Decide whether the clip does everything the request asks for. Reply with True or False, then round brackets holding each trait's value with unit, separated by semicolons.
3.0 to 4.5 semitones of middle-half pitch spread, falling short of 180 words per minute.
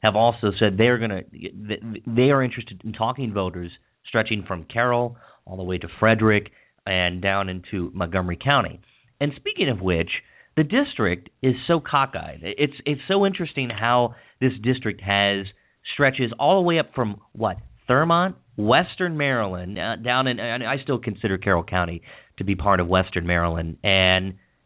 False (5.5 semitones; 165 wpm)